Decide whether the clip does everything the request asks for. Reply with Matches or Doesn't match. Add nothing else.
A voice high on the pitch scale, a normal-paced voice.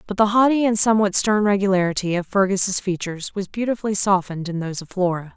Matches